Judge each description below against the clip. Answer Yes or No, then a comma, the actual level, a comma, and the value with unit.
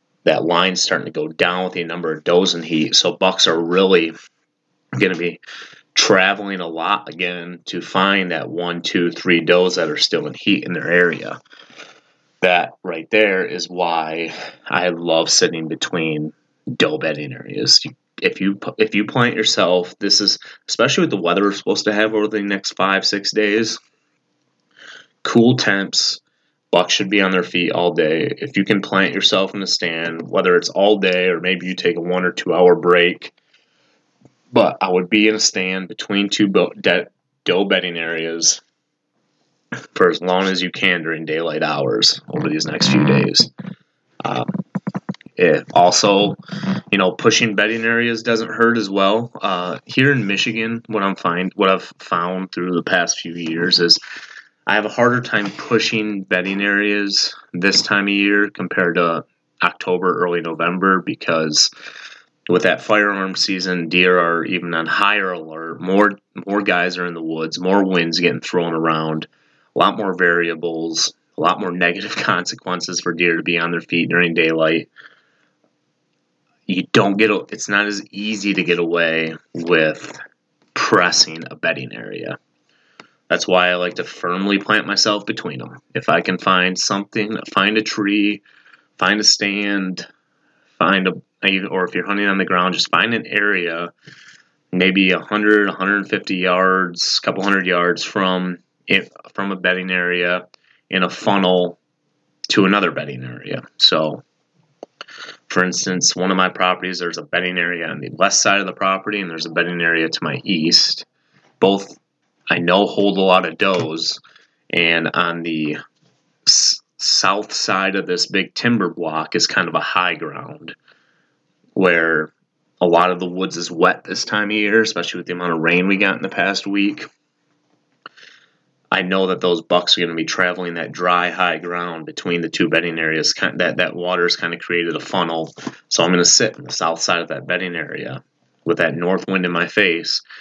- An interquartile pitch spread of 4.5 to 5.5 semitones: No, average, 2.7 semitones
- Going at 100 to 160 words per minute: No, average, 175 wpm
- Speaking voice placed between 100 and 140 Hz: No, very low, 90 Hz